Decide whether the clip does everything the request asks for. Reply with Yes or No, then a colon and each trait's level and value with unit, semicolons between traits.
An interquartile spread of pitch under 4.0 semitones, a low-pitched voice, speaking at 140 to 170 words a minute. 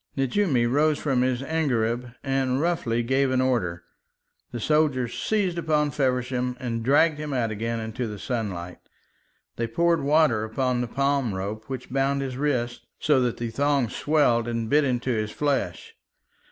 Yes: average, 3.6 semitones; low, 130 Hz; average, 160 wpm